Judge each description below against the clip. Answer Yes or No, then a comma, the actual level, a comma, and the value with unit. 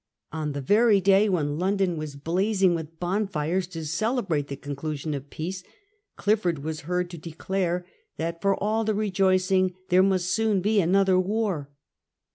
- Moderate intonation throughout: Yes, average, 3.7 semitones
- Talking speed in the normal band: Yes, average, 155 wpm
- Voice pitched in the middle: Yes, medium, 180 Hz